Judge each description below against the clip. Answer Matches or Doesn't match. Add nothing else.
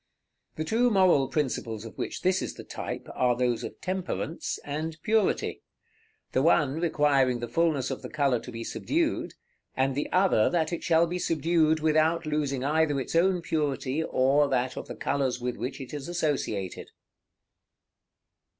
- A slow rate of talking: Doesn't match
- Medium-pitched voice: Matches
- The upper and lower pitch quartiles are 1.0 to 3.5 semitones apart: Doesn't match